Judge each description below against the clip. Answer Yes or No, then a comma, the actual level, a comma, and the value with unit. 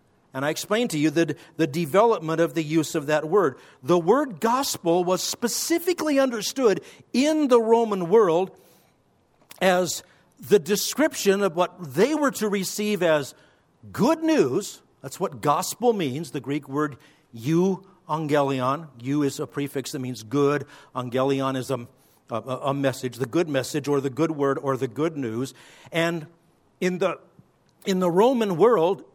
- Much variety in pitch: Yes, wide, 6.2 semitones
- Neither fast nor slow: Yes, average, 155 wpm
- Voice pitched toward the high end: No, medium, 165 Hz